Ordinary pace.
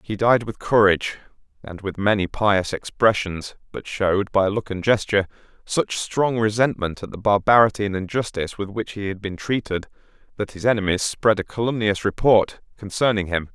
Yes: average, 170 wpm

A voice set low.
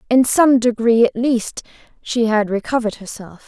No: high, 235 Hz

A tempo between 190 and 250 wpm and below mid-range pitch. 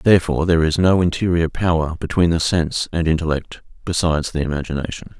No: average, 160 wpm; very low, 80 Hz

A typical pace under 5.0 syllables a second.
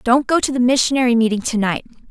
No: 6.8 syllables/s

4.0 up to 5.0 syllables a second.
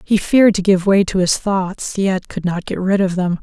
Yes: 4.9 syllables/s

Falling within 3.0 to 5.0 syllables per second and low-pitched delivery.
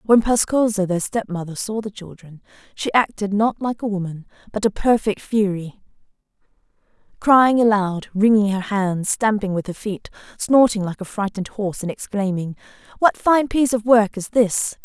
No: 4.9 syllables/s; high, 210 Hz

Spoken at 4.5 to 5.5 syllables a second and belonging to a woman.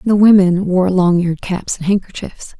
Yes: 4.8 syllables/s; female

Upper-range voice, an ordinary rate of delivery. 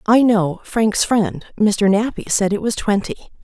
Yes: high, 210 Hz; average, 175 wpm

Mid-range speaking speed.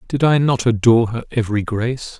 Yes: average, 190 wpm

